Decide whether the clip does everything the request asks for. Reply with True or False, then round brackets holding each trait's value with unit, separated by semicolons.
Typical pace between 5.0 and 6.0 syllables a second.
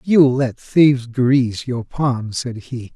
False (3.5 syllables/s)